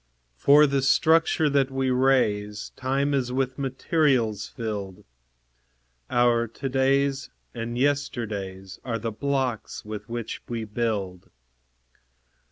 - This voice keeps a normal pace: No, slow, 110 wpm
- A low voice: Yes, low, 125 Hz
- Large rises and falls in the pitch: No, average, 3.9 semitones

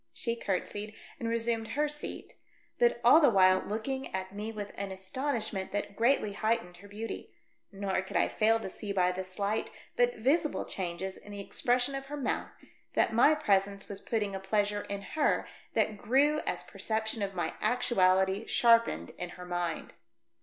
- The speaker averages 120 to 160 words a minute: No, average, 175 wpm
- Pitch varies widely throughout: No, average, 3.5 semitones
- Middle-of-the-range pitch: No, high, 210 Hz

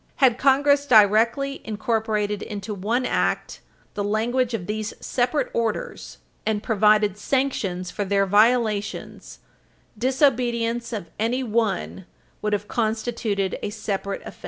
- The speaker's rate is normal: No, slow, 120 wpm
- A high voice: Yes, high, 220 Hz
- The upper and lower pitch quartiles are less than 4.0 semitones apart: Yes, average, 2.8 semitones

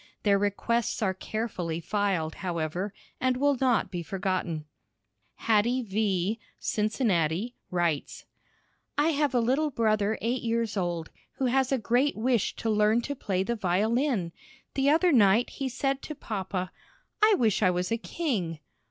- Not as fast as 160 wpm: Yes, average, 150 wpm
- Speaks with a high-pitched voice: Yes, high, 215 Hz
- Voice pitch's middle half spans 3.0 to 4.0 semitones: No, average, 5.3 semitones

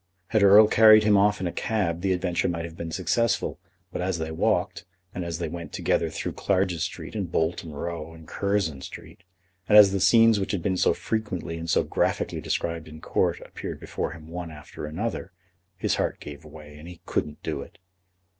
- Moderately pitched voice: No, very low, 85 Hz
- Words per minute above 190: Yes, average, 200 wpm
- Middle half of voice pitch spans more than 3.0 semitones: Yes, average, 3.6 semitones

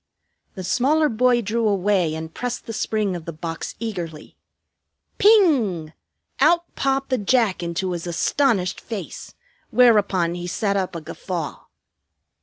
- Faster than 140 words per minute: No, slow, 135 wpm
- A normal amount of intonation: No, wide, 6.1 semitones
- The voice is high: Yes, high, 200 Hz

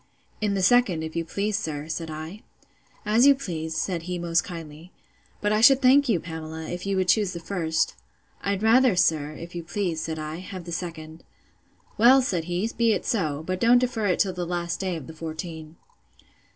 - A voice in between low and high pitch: Yes, medium, 175 Hz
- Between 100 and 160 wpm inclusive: No, average, 200 wpm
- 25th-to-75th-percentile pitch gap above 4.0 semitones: Yes, average, 4.4 semitones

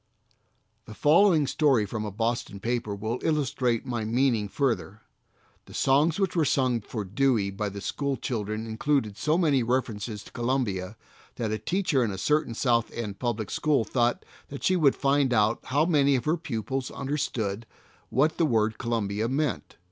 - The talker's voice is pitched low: Yes, low, 120 Hz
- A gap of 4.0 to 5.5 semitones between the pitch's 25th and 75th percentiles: Yes, average, 4.6 semitones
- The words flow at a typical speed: Yes, average, 170 wpm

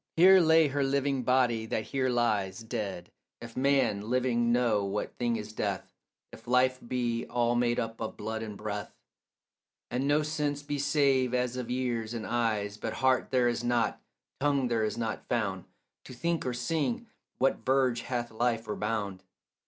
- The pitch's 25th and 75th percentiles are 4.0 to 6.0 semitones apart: No, average, 2.8 semitones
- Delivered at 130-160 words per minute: No, average, 175 wpm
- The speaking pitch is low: Yes, low, 120 Hz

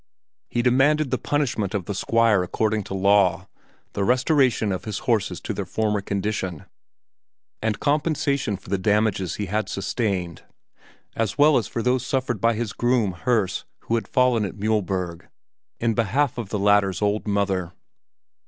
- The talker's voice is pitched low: Yes, low, 105 Hz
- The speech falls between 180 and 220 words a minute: No, average, 160 wpm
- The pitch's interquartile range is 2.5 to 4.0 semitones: Yes, average, 3.7 semitones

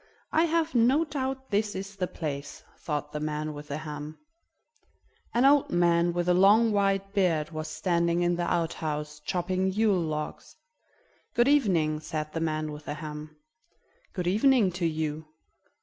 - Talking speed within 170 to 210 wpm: No, average, 160 wpm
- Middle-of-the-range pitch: Yes, medium, 175 Hz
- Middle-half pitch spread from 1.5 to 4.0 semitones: No, average, 4.7 semitones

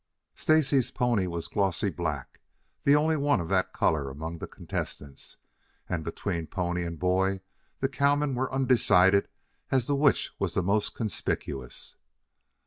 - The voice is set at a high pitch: No, low, 100 Hz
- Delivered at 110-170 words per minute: Yes, average, 145 wpm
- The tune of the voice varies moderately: No, wide, 7.8 semitones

